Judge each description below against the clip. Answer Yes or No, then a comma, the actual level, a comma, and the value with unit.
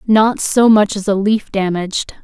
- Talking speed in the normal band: Yes, average, 190 wpm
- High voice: Yes, high, 205 Hz